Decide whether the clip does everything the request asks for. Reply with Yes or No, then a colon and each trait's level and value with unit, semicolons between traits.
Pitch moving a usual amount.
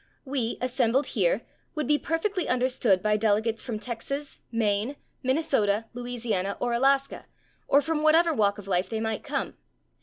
Yes: average, 4.5 semitones